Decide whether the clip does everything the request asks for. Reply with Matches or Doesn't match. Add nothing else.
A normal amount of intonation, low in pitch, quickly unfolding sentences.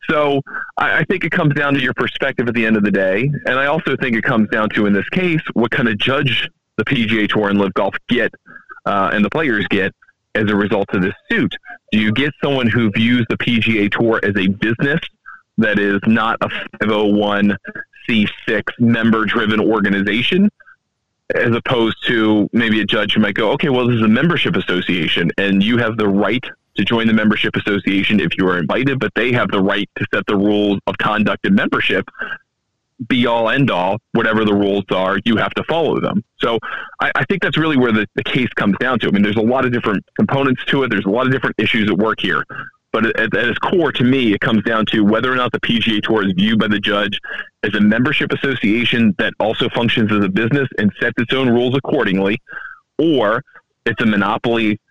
Matches